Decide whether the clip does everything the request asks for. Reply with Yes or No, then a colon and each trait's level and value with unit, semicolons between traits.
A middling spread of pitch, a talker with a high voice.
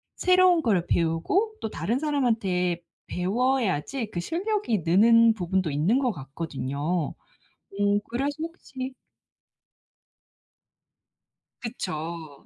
No: wide, 7.7 semitones; high, 205 Hz